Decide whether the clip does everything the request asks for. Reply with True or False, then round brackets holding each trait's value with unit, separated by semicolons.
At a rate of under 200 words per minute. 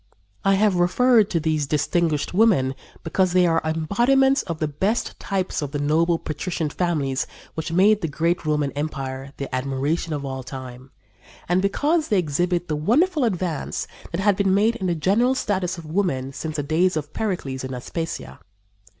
True (175 wpm)